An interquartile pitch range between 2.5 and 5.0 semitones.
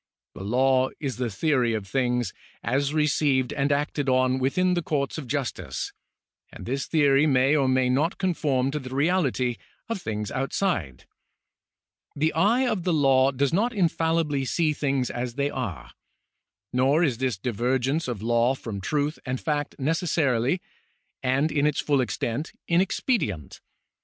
Yes: average, 3.4 semitones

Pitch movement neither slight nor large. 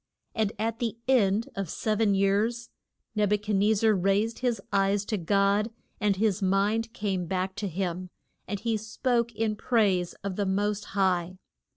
No: narrow, 2.2 semitones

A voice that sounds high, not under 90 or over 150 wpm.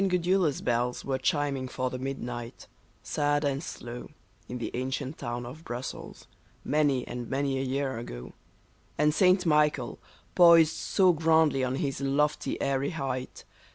No: low, 135 Hz; average, 145 wpm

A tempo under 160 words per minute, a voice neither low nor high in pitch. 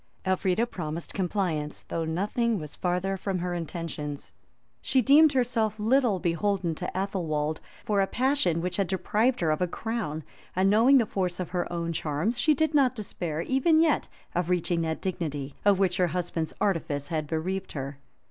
No: average, 175 wpm; medium, 180 Hz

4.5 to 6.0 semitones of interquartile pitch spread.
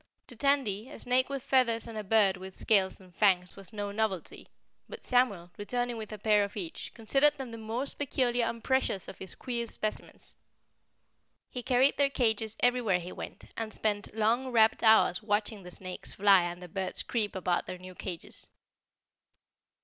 No: average, 4.1 semitones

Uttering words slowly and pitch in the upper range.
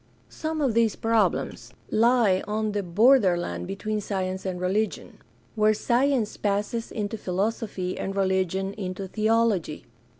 Yes: slow, 125 wpm; high, 210 Hz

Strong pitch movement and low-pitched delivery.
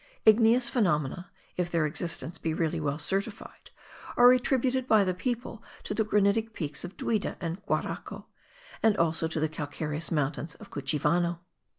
No: wide, 5.9 semitones; medium, 175 Hz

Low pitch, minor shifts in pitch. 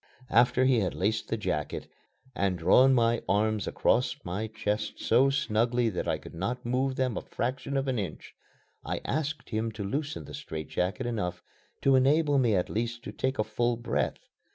No: low, 120 Hz; average, 4.0 semitones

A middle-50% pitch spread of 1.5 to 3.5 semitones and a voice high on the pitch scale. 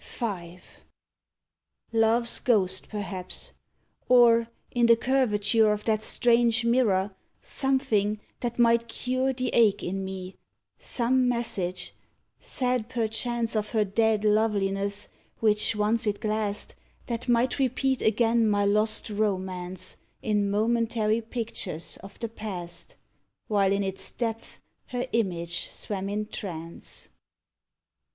Yes: average, 2.8 semitones; high, 215 Hz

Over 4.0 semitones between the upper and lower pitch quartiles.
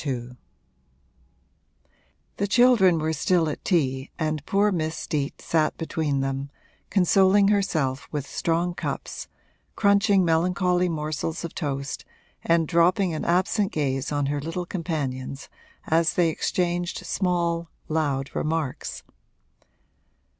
No: average, 3.7 semitones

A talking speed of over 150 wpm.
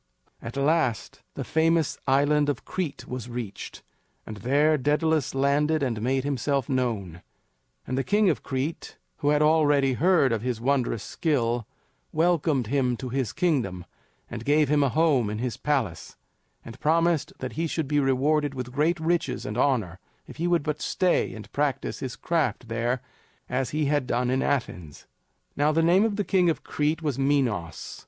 Yes: average, 175 wpm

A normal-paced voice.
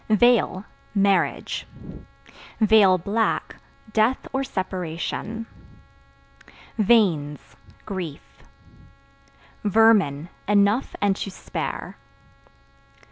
No: slow, 60 wpm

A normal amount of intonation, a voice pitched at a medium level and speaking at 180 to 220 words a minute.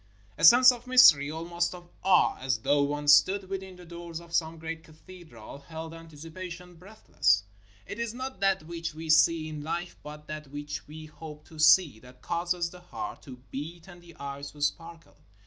Yes: average, 3.1 semitones; medium, 165 Hz; average, 190 wpm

